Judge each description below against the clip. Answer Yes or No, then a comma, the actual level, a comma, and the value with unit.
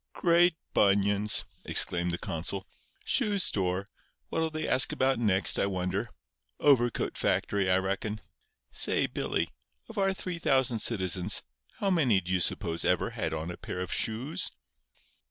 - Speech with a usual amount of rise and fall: No, wide, 7.2 semitones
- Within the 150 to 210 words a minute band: No, slow, 135 wpm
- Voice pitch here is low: Yes, low, 105 Hz